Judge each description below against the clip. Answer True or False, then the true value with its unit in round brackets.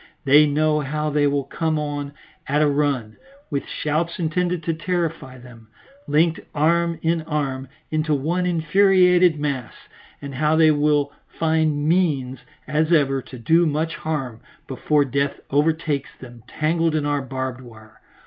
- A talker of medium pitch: True (150 Hz)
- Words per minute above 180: False (150 wpm)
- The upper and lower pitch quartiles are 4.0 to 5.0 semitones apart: False (2.7 semitones)